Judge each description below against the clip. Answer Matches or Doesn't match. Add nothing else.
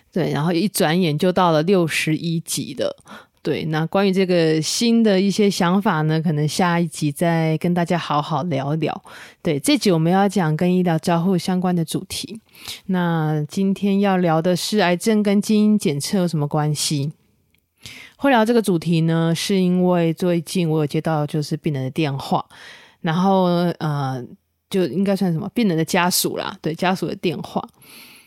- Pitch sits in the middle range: Matches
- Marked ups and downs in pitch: Doesn't match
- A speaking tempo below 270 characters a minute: Matches